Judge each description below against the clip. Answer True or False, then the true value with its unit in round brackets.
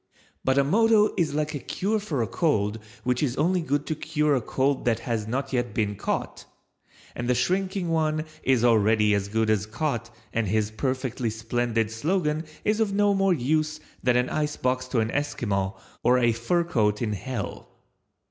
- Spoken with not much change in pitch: False (5.5 semitones)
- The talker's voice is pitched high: False (130 Hz)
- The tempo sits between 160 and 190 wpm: True (185 wpm)